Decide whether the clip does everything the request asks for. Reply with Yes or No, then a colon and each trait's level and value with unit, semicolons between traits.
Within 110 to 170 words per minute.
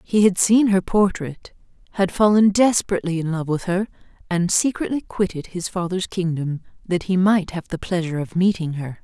No: average, 180 wpm